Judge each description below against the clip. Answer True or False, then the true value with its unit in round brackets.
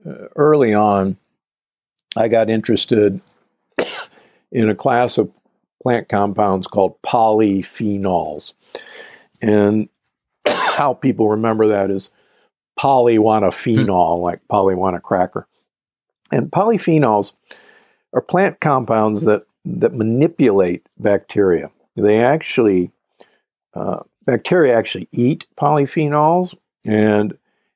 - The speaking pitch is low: True (110 Hz)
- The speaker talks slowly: True (90 wpm)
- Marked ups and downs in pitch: False (4.6 semitones)